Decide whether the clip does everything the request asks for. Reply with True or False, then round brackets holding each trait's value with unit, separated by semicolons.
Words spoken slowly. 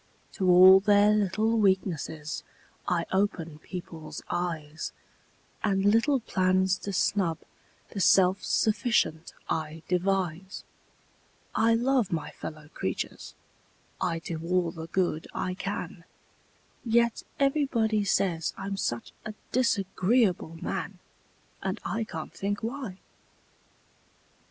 True (110 wpm)